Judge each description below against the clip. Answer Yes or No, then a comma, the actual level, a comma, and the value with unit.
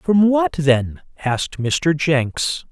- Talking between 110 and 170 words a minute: Yes, slow, 135 wpm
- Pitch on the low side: No, medium, 155 Hz